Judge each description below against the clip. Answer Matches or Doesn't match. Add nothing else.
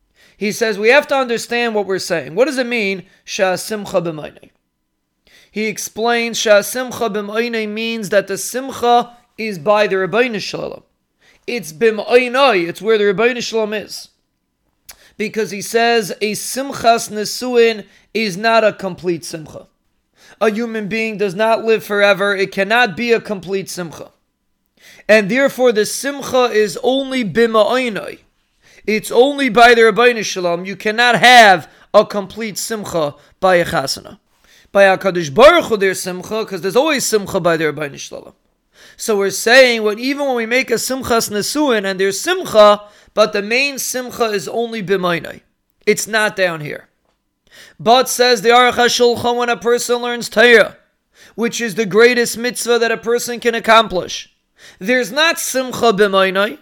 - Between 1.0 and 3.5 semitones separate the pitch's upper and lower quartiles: Matches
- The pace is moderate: Matches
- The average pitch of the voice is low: Doesn't match